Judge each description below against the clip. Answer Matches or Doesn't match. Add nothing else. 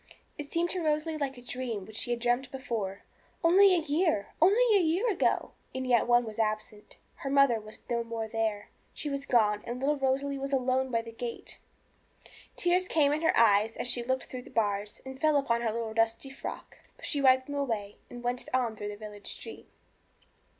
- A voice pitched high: Matches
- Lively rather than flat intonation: Doesn't match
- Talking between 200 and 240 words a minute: Matches